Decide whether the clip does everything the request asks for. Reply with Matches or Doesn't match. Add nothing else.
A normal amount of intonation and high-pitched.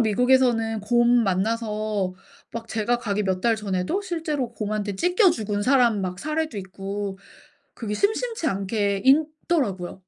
Matches